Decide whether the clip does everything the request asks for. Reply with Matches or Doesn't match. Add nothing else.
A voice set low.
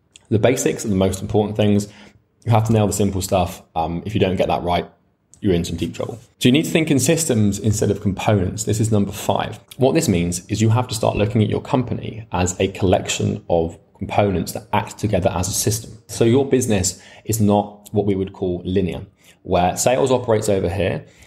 Matches